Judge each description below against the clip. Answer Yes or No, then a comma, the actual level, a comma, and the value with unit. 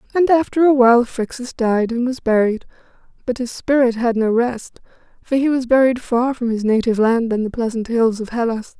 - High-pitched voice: Yes, high, 240 Hz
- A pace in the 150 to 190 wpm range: No, average, 200 wpm